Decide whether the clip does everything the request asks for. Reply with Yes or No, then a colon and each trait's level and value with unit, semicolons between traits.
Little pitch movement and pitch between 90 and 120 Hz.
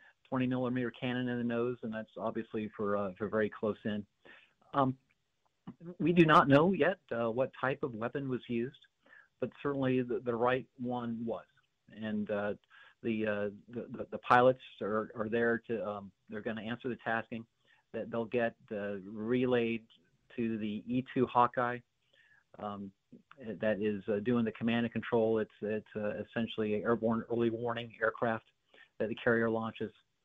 Yes: narrow, 2.3 semitones; low, 115 Hz